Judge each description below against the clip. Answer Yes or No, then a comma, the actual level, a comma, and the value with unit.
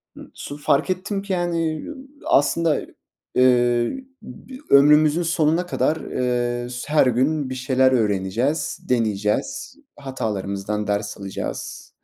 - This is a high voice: No, low, 130 Hz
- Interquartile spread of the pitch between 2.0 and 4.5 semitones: No, average, 4.9 semitones